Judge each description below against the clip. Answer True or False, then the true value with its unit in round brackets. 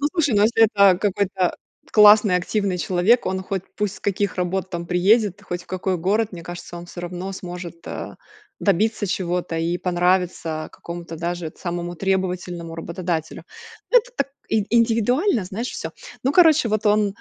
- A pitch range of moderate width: True (3.1 semitones)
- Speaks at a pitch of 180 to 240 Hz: True (190 Hz)